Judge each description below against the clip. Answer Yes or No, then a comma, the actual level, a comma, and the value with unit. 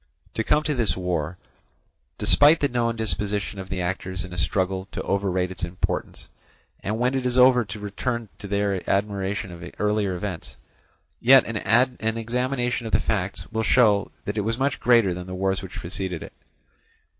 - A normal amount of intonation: Yes, average, 4.0 semitones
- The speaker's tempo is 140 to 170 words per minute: No, average, 180 wpm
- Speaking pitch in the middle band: No, low, 105 Hz